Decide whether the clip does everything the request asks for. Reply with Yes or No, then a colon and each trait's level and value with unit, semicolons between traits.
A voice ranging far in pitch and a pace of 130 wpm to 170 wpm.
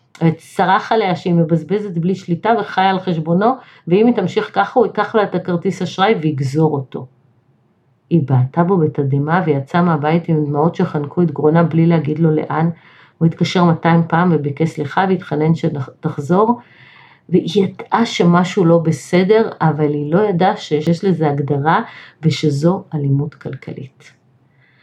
No: average, 3.8 semitones; average, 145 wpm